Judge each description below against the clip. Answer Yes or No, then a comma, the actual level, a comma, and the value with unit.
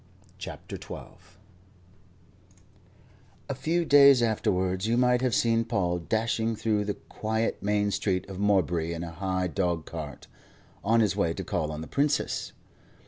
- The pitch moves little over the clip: No, average, 4.5 semitones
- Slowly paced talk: No, average, 145 wpm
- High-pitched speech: No, low, 105 Hz